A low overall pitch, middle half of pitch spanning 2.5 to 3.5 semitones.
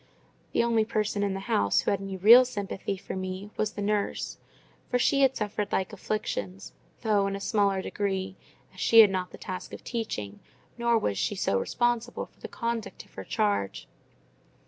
No: high, 205 Hz; average, 3.0 semitones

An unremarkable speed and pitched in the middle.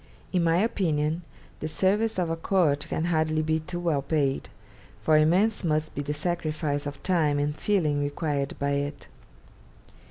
Yes: average, 160 wpm; medium, 155 Hz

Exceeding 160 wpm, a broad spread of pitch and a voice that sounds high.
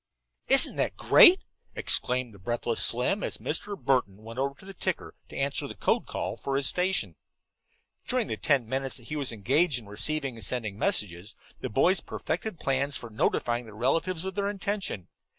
No: average, 185 wpm; wide, 7.5 semitones; low, 135 Hz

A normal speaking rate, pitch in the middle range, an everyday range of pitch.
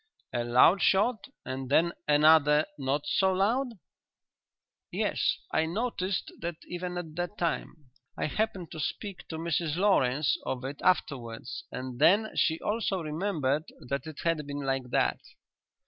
Yes: average, 145 wpm; medium, 160 Hz; average, 4.8 semitones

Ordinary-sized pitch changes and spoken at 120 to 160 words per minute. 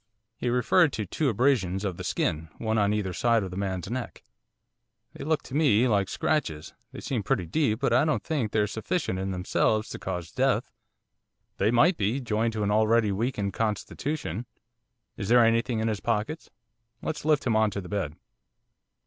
No: average, 4.0 semitones; average, 185 wpm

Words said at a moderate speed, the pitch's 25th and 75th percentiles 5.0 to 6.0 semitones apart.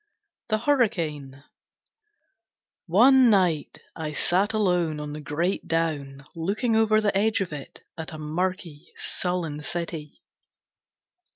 No: slow, 115 wpm; average, 5.3 semitones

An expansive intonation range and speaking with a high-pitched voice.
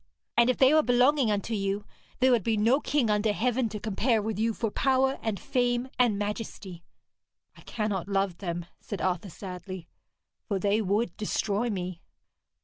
No: average, 3.6 semitones; high, 215 Hz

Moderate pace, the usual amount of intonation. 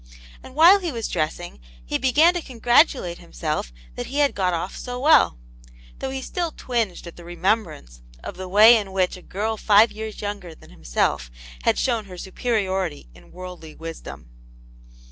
No: average, 170 wpm; wide, 6.0 semitones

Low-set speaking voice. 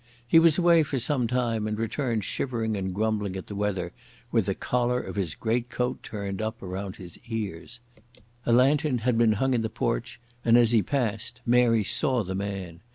Yes: low, 115 Hz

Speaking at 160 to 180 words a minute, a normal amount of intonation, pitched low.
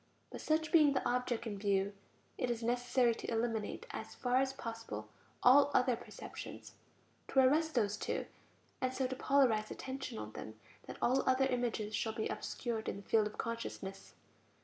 No: average, 170 wpm; average, 3.1 semitones; high, 240 Hz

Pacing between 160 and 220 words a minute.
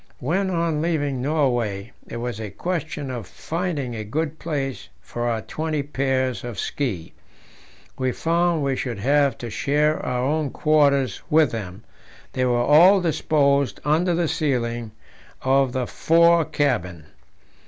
No: average, 145 wpm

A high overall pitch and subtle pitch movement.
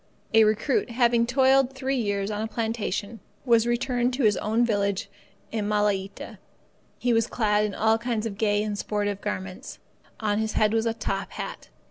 Yes: high, 220 Hz; narrow, 2.3 semitones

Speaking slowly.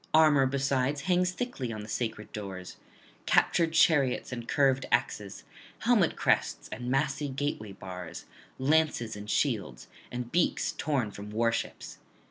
Yes: slow, 130 wpm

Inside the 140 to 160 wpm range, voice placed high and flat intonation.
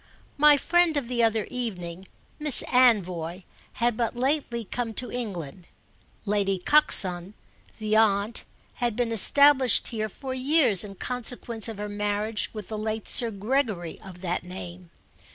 No: average, 145 wpm; high, 220 Hz; average, 4.2 semitones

